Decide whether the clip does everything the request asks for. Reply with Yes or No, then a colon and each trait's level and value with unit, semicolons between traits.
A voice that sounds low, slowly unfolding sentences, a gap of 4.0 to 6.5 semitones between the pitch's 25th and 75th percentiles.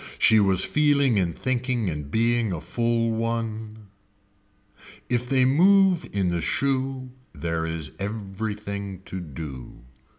Yes: low, 110 Hz; slow, 125 wpm; wide, 5.4 semitones